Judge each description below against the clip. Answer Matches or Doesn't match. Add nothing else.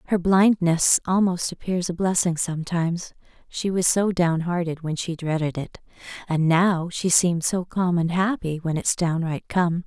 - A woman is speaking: Matches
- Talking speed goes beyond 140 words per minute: Matches